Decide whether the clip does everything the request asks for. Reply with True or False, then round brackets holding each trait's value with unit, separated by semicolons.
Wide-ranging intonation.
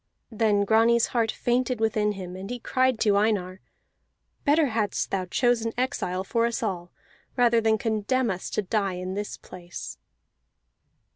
False (3.4 semitones)